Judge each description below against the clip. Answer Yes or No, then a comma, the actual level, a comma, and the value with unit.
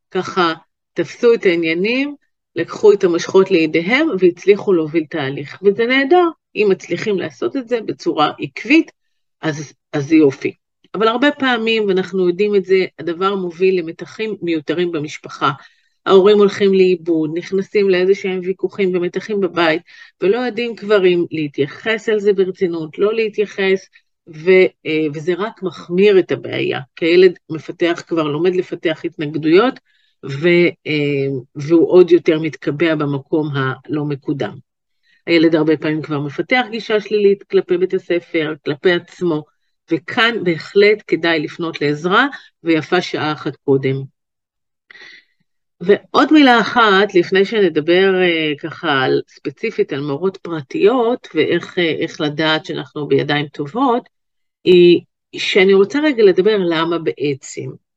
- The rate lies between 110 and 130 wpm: Yes, average, 120 wpm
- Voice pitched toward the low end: No, medium, 185 Hz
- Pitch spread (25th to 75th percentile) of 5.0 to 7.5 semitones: Yes, average, 5.3 semitones